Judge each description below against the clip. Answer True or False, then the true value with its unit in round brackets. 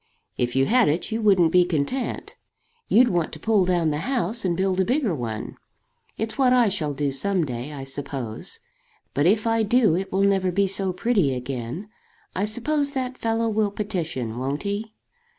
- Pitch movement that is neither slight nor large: False (7.1 semitones)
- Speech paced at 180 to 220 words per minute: True (185 wpm)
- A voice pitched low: False (190 Hz)